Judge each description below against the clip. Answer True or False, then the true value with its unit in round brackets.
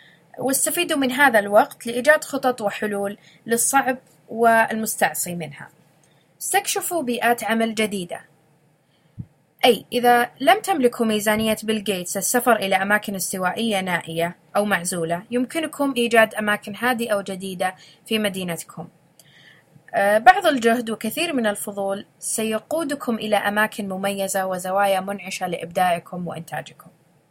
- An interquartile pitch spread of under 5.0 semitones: False (5.5 semitones)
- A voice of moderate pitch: False (205 Hz)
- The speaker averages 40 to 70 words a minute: False (105 wpm)